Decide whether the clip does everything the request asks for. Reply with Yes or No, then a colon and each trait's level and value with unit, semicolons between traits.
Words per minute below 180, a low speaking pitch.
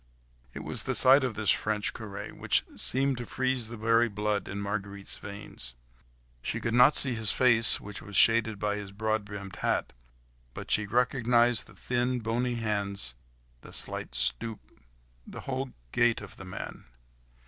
Yes: average, 165 wpm; low, 110 Hz